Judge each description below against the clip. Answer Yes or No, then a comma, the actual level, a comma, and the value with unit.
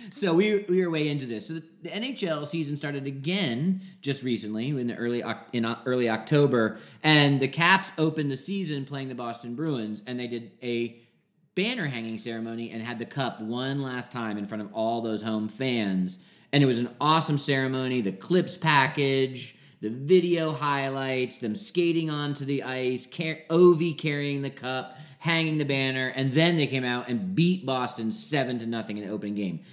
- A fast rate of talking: No, average, 190 wpm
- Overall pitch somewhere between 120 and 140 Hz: Yes, low, 135 Hz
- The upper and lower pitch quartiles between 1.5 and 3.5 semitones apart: No, average, 5.0 semitones